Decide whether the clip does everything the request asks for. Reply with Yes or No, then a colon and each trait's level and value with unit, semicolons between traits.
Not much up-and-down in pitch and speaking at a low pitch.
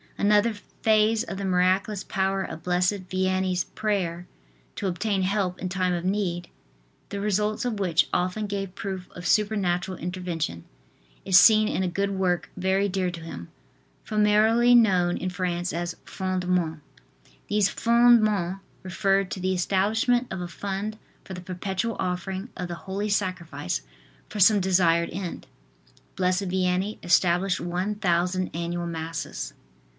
No: narrow, 2.3 semitones; medium, 185 Hz